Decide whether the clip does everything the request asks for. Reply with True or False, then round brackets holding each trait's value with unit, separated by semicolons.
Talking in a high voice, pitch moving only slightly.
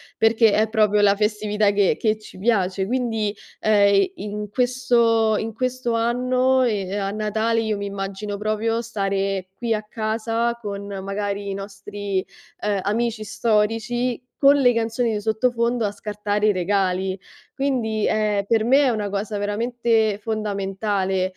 True (215 Hz; 2.3 semitones)